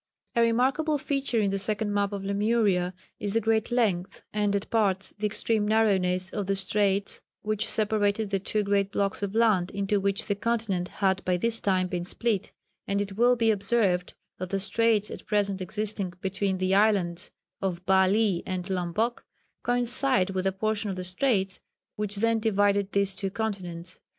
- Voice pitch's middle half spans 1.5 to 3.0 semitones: Yes, narrow, 2.4 semitones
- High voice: Yes, high, 200 Hz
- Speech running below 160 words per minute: No, average, 175 wpm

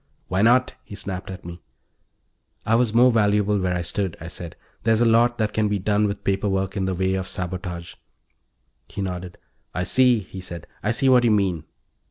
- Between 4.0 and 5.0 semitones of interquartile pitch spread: No, average, 3.1 semitones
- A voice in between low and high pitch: No, low, 100 Hz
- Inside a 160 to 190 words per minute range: No, fast, 205 wpm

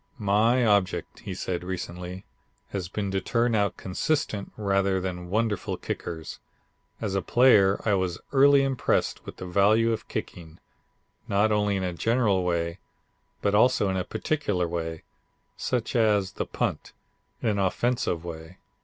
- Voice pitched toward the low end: Yes, low, 100 Hz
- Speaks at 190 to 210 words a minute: No, average, 150 wpm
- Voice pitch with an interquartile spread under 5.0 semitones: Yes, average, 3.6 semitones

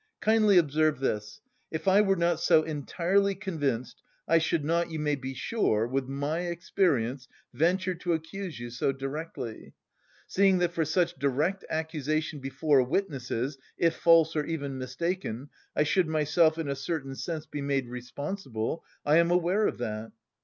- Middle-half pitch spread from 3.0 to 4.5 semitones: Yes, average, 4.1 semitones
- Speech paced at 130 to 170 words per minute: Yes, average, 160 wpm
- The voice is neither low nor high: Yes, medium, 155 Hz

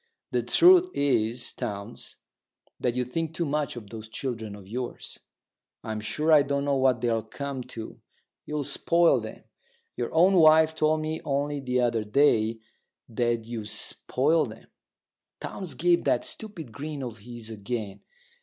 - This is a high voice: No, low, 130 Hz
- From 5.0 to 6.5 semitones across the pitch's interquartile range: Yes, wide, 5.4 semitones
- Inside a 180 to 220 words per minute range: No, average, 155 wpm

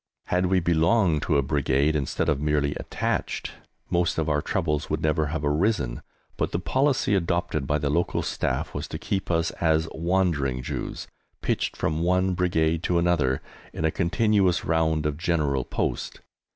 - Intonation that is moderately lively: Yes, average, 3.1 semitones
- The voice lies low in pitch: Yes, very low, 80 Hz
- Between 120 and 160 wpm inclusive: No, average, 170 wpm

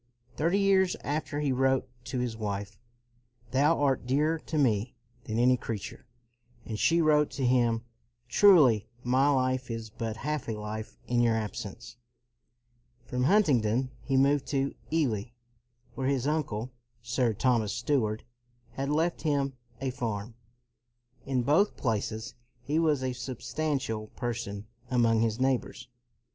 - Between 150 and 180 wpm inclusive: No, average, 140 wpm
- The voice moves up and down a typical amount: Yes, average, 3.9 semitones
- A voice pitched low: Yes, low, 125 Hz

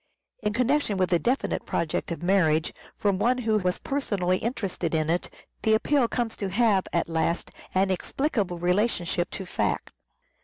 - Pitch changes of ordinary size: Yes, average, 4.6 semitones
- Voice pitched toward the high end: Yes, high, 195 Hz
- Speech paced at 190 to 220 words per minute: No, average, 160 wpm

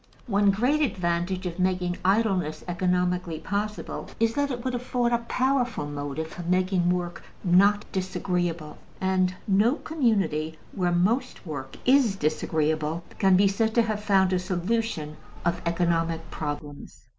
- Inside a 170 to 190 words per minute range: No, average, 140 wpm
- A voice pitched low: No, medium, 185 Hz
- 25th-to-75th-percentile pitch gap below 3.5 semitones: No, average, 4.2 semitones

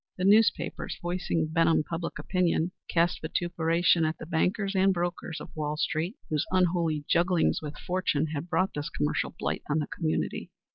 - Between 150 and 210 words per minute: Yes, average, 160 wpm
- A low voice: No, medium, 165 Hz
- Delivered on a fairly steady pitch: Yes, narrow, 2.3 semitones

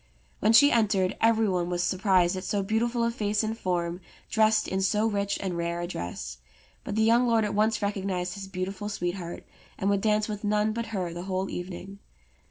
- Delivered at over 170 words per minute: Yes, average, 200 wpm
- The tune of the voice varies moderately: Yes, average, 3.0 semitones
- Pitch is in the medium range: No, high, 200 Hz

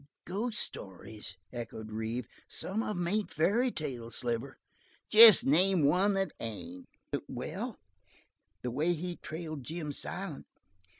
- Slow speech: Yes, slow, 125 wpm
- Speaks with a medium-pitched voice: Yes, medium, 155 Hz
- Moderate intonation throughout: No, wide, 8.5 semitones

